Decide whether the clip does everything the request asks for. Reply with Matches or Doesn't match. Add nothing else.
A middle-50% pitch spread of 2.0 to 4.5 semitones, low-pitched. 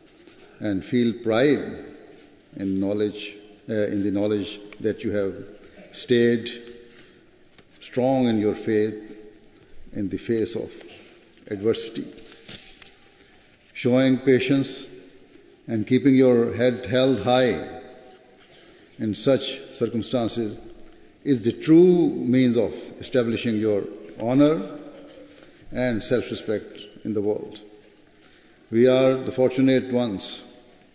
Matches